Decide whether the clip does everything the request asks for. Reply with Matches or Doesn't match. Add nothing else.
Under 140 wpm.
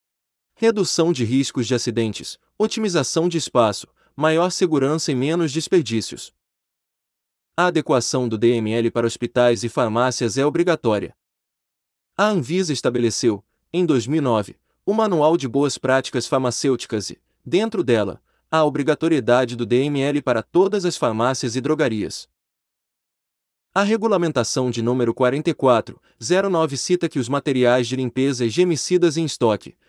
Matches